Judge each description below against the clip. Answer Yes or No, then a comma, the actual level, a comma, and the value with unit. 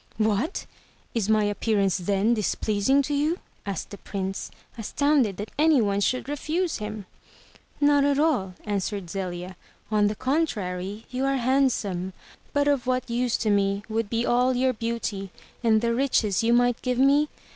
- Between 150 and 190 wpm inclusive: Yes, average, 160 wpm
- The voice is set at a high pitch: Yes, high, 230 Hz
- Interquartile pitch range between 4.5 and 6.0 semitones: Yes, average, 4.8 semitones